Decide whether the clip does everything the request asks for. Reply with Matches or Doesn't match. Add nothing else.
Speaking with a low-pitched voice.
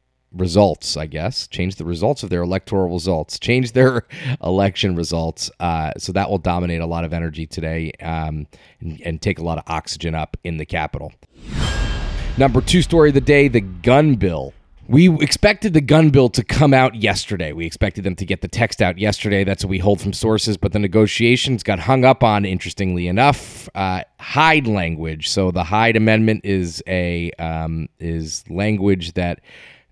Matches